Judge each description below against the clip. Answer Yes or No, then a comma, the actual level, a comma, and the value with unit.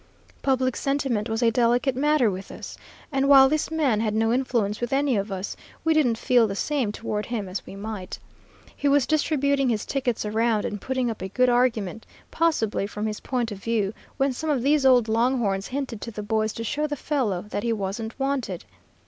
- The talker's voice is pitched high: Yes, high, 235 Hz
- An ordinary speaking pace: No, fast, 210 wpm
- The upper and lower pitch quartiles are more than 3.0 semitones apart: Yes, average, 4.2 semitones